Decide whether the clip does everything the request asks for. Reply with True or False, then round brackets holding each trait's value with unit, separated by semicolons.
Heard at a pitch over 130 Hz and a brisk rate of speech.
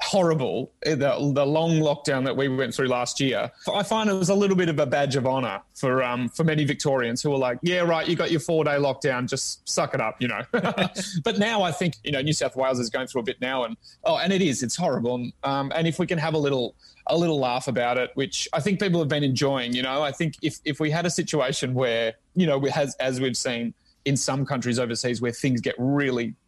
True (140 Hz; 245 wpm)